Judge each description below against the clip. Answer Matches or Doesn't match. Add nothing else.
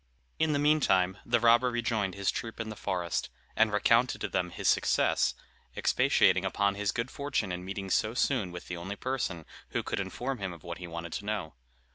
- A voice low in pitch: Matches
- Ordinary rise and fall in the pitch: Matches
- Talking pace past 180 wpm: Matches